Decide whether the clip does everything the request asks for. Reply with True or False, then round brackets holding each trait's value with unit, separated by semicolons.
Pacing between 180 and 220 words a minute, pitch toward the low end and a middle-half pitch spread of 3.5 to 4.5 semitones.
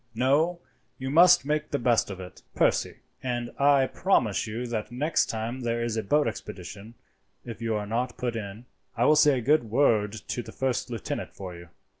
True (200 wpm; 120 Hz; 3.9 semitones)